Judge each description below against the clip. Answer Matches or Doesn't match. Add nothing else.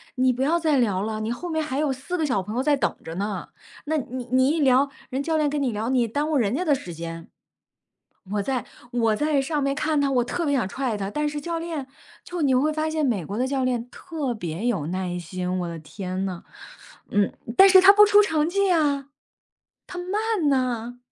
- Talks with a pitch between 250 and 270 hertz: Matches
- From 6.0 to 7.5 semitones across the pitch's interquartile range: Matches